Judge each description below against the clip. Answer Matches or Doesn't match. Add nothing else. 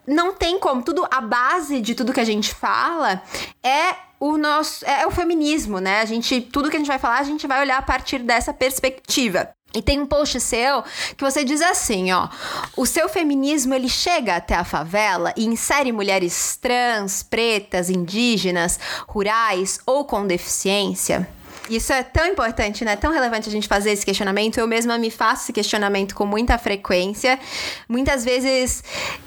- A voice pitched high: Matches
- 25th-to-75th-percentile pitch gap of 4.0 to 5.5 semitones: Matches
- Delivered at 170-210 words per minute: Matches